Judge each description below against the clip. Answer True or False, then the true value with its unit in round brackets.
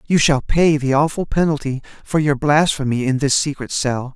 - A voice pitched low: False (145 Hz)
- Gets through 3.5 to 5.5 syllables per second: True (5.0 syllables/s)